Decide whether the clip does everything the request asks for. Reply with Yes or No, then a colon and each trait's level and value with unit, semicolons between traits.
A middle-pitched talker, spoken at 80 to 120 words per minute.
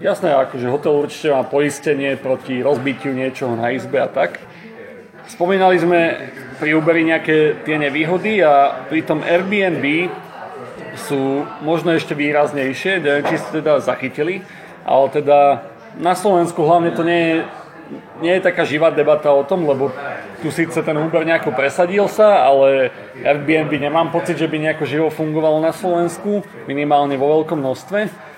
No: medium, 155 Hz; average, 150 wpm